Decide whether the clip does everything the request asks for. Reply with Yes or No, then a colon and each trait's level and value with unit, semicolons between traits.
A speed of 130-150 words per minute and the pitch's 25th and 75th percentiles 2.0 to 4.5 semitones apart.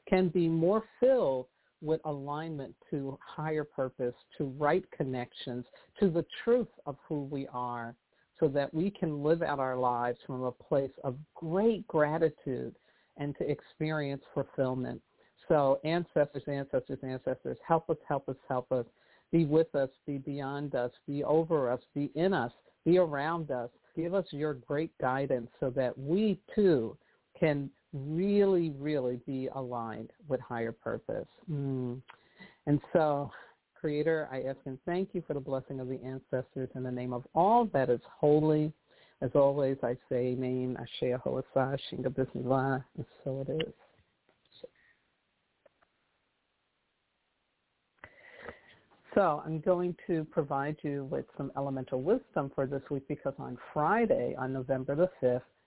Yes: average, 145 wpm; average, 3.7 semitones